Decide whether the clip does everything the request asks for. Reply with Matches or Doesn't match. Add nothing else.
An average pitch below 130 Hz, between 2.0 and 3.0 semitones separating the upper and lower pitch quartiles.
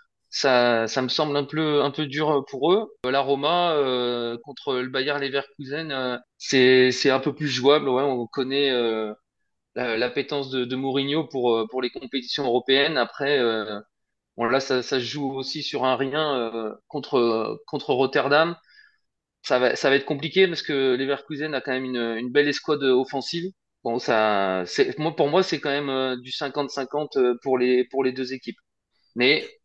Doesn't match